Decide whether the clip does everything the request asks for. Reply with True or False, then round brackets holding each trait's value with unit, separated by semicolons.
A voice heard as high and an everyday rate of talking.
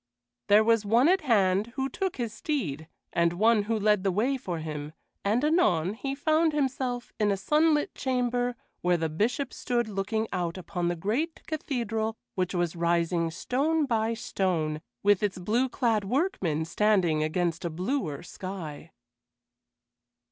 True (210 Hz; 155 wpm)